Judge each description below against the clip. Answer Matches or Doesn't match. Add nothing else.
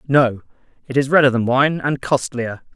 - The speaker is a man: Matches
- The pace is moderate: Matches